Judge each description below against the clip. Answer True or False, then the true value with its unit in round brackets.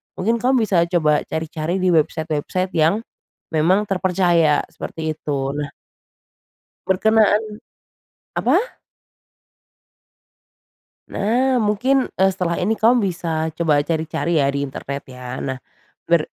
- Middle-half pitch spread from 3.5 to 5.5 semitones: True (5.0 semitones)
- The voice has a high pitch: False (170 Hz)